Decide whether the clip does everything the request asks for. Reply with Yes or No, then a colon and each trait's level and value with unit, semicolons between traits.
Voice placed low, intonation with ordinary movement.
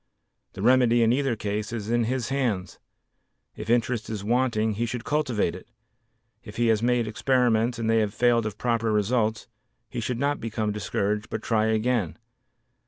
No: low, 115 Hz; narrow, 2.2 semitones